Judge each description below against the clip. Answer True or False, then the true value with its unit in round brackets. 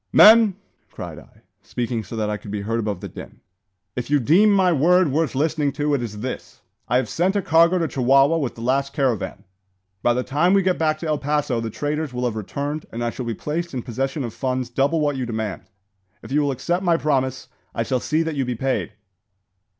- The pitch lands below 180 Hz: True (135 Hz)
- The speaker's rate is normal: False (225 wpm)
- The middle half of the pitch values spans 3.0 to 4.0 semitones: False (4.8 semitones)